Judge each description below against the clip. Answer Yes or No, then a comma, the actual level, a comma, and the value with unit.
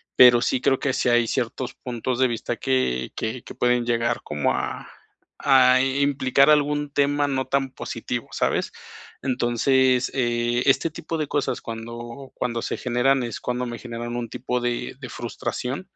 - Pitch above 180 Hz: No, low, 125 Hz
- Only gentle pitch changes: Yes, narrow, 2.2 semitones